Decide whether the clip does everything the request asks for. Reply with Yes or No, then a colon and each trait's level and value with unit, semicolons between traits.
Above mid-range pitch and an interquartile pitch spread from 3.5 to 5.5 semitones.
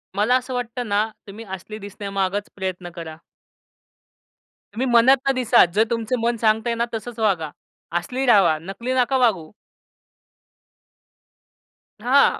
Yes: high, 225 Hz; average, 4.0 semitones